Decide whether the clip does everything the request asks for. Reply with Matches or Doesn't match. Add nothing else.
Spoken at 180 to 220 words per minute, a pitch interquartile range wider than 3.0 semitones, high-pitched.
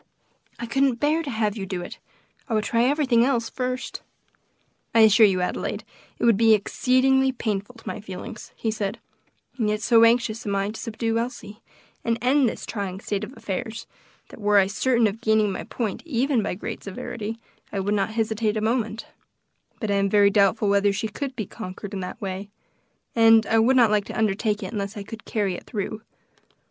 Doesn't match